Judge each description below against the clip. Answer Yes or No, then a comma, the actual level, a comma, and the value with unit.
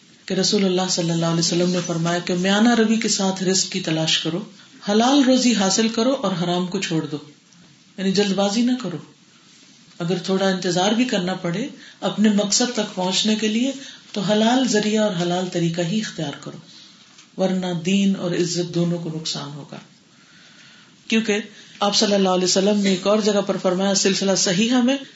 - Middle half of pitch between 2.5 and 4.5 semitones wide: Yes, average, 3.1 semitones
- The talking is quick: No, average, 180 wpm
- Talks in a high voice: Yes, high, 195 Hz